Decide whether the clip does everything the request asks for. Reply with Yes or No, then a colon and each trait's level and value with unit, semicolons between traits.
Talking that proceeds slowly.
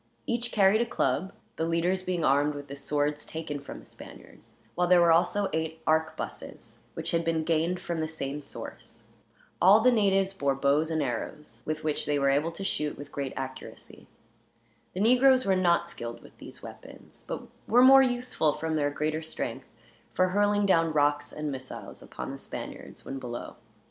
No: average, 185 wpm